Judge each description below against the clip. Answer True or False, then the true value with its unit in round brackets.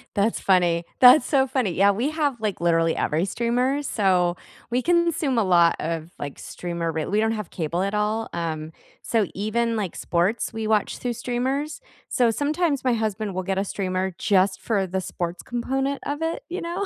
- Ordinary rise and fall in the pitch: False (5.9 semitones)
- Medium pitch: False (215 Hz)